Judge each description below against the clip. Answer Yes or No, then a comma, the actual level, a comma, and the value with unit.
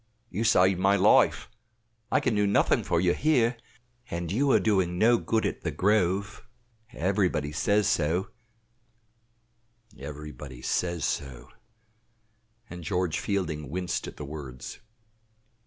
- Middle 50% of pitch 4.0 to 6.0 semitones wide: Yes, average, 4.9 semitones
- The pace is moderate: No, slow, 125 wpm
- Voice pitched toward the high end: No, very low, 90 Hz